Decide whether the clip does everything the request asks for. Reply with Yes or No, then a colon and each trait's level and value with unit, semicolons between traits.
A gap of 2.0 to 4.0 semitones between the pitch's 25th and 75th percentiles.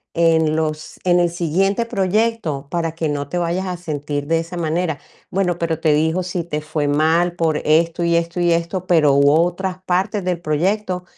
Yes: narrow, 2.5 semitones